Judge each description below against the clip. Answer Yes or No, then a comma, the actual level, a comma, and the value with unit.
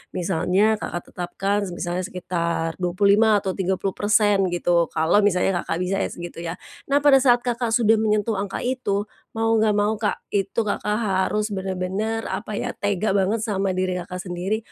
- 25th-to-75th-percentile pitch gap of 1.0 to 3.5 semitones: Yes, average, 2.9 semitones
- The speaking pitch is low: No, high, 200 Hz